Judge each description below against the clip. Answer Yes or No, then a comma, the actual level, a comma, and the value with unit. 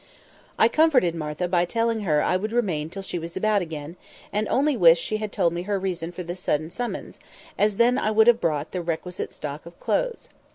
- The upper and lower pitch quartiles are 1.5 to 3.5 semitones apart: No, average, 4.6 semitones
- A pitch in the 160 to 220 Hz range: Yes, medium, 185 Hz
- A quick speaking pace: Yes, fast, 215 wpm